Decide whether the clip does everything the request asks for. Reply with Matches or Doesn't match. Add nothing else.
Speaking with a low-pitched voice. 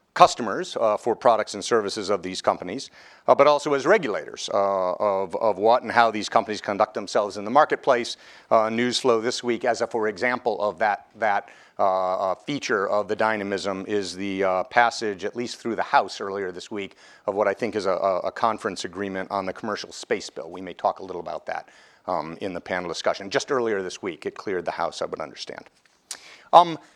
Matches